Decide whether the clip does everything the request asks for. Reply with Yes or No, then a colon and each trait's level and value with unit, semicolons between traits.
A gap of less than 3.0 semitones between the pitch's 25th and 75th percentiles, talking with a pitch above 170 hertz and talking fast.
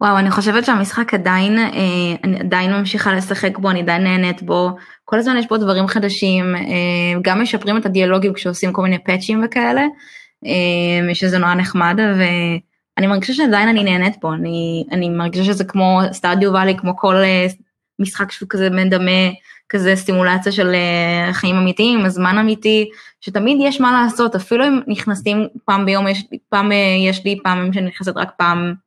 Yes: narrow, 2.4 semitones; high, 190 Hz; fast, 160 wpm